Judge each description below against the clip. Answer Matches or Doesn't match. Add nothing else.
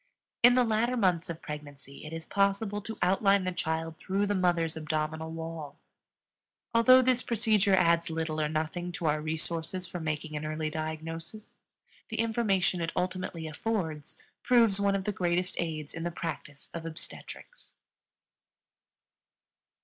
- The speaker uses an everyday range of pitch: Matches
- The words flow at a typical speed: Matches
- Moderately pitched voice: Matches